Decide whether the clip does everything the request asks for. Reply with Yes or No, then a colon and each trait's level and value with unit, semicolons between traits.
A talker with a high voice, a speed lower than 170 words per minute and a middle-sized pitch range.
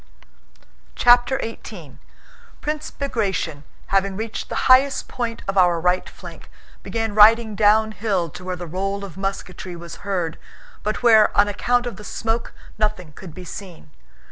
Yes: high, 205 Hz; average, 145 wpm; average, 3.7 semitones